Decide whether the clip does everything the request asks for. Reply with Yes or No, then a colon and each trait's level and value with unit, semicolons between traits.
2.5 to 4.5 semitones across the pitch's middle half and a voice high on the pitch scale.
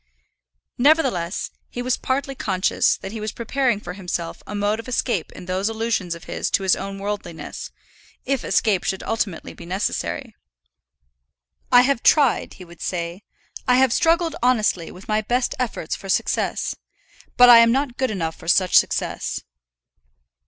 No: average, 5.1 semitones; high, 215 Hz